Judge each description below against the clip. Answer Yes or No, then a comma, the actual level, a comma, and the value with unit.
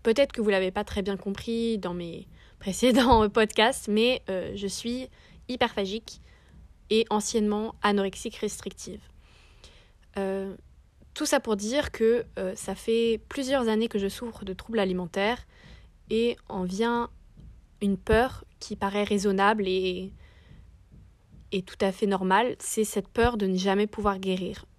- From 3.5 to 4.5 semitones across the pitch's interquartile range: No, average, 2.9 semitones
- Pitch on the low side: No, high, 205 Hz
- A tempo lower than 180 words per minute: Yes, average, 150 wpm